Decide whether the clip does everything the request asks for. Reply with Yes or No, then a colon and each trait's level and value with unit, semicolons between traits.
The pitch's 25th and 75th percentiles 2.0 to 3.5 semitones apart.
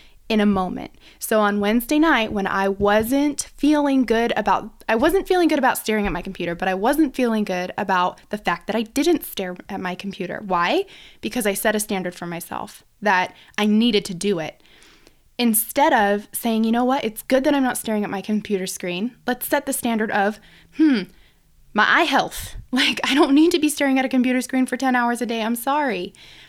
No: average, 4.8 semitones